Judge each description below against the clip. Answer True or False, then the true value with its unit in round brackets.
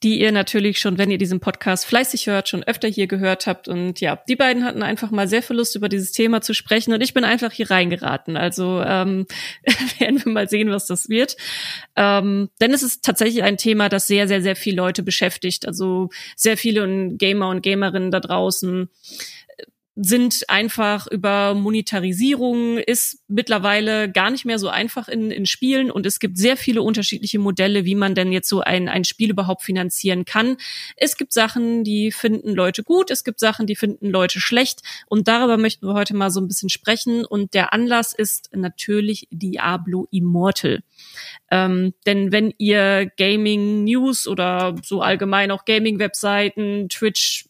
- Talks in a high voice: True (205 Hz)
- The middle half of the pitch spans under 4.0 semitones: True (2.9 semitones)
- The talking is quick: False (180 wpm)